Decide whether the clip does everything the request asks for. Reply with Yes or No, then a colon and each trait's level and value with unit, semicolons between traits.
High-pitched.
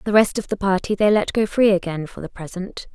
Yes: high, 195 Hz